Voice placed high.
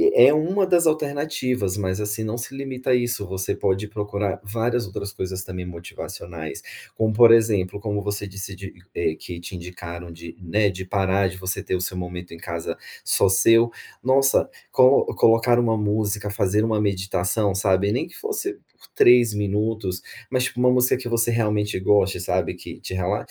No: low, 105 Hz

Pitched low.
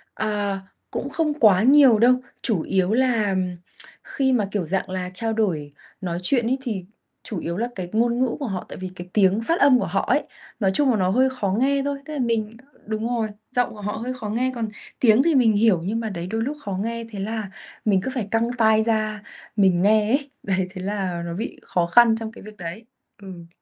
No: high, 220 Hz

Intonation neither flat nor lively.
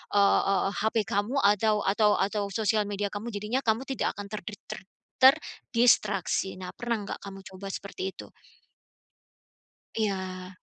No: narrow, 2.0 semitones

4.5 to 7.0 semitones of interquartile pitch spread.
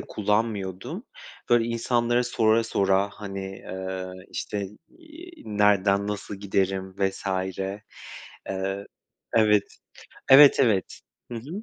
No: average, 3.3 semitones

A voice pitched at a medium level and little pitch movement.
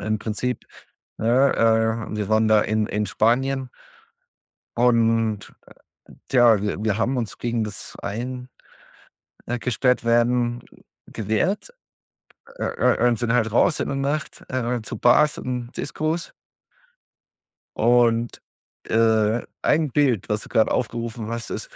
No: low, 115 Hz; narrow, 2.3 semitones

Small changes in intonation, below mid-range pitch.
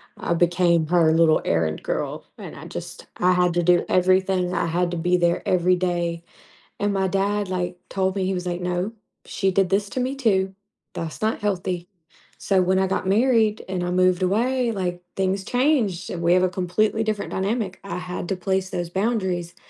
No: narrow, 1.9 semitones; medium, 185 Hz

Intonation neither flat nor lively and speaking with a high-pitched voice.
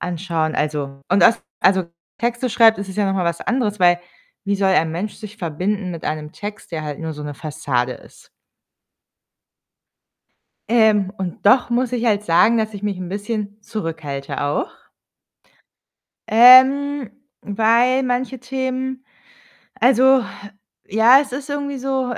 No: wide, 6.4 semitones; high, 210 Hz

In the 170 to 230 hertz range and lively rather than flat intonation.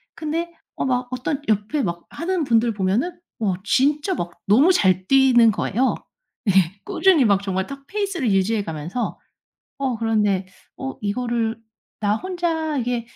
No: high, 240 Hz; wide, 6.4 semitones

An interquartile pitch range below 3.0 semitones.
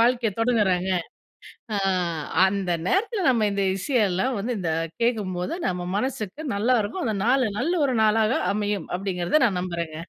No: average, 4.8 semitones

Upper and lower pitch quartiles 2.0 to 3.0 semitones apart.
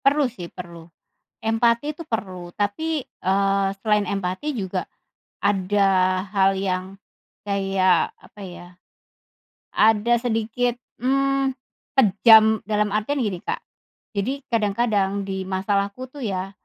No: average, 3.6 semitones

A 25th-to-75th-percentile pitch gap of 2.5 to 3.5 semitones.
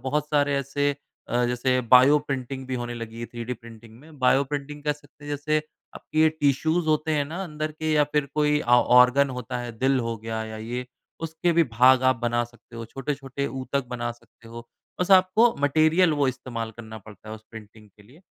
No: average, 3.9 semitones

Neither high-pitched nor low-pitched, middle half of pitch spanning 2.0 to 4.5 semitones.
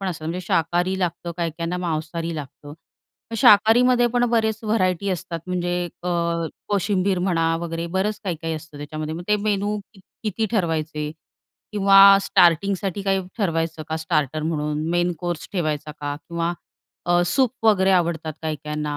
Yes: medium, 175 Hz; average, 3.6 semitones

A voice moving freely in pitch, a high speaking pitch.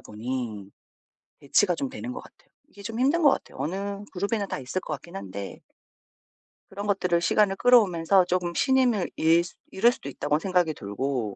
No: wide, 6.6 semitones; medium, 180 Hz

